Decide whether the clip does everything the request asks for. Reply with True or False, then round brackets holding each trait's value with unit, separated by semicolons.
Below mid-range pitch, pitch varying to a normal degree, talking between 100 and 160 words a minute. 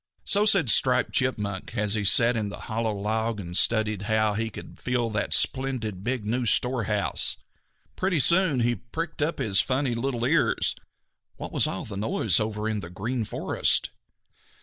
False (115 Hz; 3.5 semitones; 170 wpm)